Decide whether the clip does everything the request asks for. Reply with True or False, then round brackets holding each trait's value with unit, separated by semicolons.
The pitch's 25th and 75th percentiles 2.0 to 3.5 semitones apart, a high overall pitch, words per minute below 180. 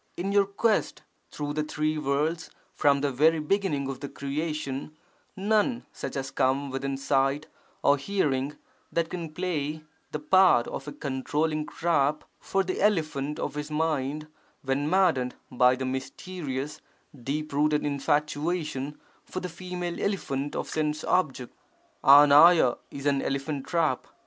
False (3.2 semitones; 150 Hz; 140 wpm)